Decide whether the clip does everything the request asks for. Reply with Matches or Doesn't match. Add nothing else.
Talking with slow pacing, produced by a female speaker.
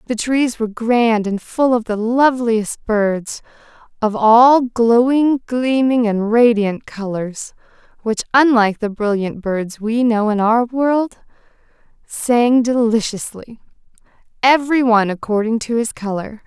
Matches